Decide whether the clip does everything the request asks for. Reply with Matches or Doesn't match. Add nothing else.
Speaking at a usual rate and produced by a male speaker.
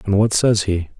Doesn't match